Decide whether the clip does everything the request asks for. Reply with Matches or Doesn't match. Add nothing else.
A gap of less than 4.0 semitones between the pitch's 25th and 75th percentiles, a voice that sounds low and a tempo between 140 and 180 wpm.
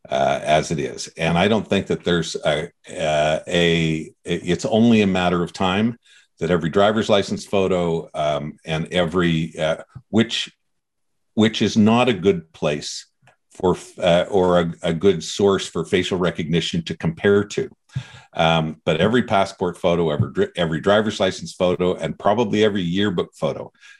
Doesn't match